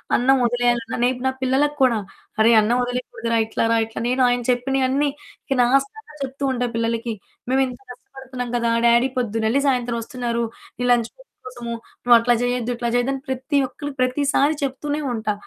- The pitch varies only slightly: Yes, narrow, 2.2 semitones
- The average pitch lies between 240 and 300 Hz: Yes, high, 245 Hz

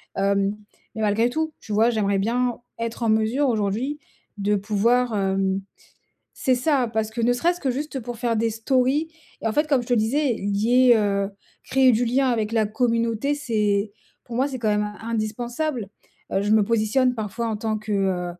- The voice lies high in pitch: Yes, high, 230 Hz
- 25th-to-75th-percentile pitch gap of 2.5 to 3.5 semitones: Yes, average, 3.1 semitones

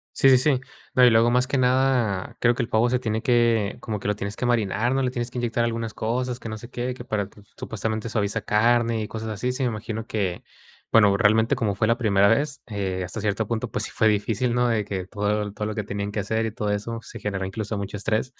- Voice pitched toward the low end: Yes, low, 110 Hz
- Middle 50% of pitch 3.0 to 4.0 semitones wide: No, narrow, 2.6 semitones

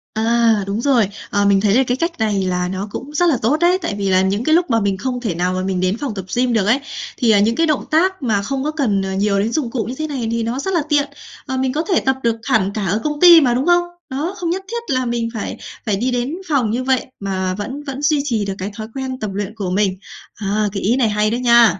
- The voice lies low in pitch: No, high, 235 Hz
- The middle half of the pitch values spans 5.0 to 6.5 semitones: Yes, average, 5.3 semitones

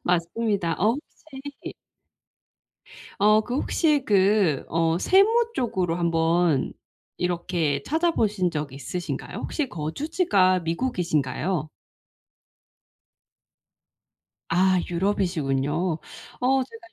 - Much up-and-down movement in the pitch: Yes, wide, 6.1 semitones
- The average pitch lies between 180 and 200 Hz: Yes, medium, 185 Hz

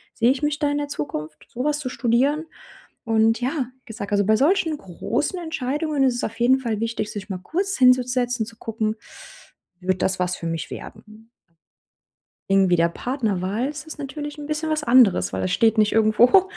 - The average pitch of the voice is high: Yes, high, 240 Hz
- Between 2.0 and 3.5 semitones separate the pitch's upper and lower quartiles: No, wide, 5.6 semitones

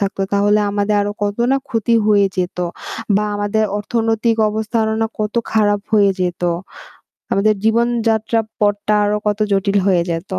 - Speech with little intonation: Yes, narrow, 1.5 semitones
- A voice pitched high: Yes, high, 210 Hz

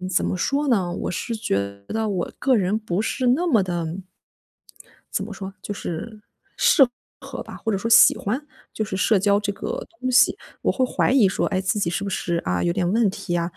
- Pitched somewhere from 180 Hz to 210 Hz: Yes, high, 200 Hz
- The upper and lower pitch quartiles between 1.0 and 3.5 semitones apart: No, average, 3.9 semitones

